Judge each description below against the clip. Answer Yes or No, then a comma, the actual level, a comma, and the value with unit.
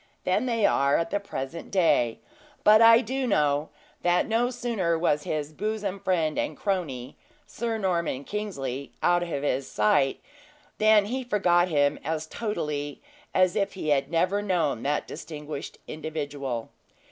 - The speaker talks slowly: No, average, 145 wpm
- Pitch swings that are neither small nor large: No, wide, 6.1 semitones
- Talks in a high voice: No, medium, 170 Hz